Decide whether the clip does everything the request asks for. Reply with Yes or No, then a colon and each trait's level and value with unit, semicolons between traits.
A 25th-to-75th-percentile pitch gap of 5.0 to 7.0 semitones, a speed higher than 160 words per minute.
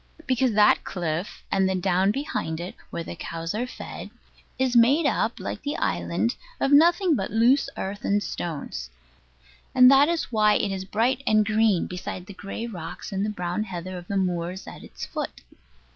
Yes: wide, 5.4 semitones; average, 180 wpm